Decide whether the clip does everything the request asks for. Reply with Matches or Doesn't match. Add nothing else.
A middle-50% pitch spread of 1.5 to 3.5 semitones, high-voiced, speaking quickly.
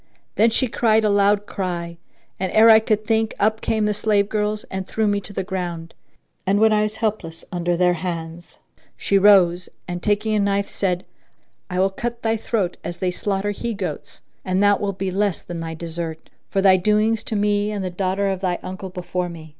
Matches